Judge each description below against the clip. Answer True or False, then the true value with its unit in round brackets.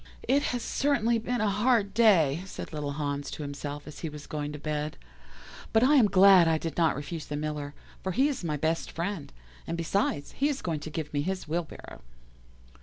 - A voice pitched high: False (165 Hz)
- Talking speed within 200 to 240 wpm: True (205 wpm)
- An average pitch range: False (6.0 semitones)